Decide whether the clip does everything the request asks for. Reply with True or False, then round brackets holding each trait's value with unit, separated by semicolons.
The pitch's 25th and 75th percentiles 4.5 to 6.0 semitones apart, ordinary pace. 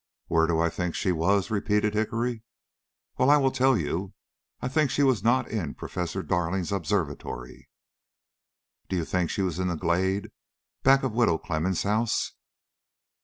True (5.2 semitones; 160 wpm)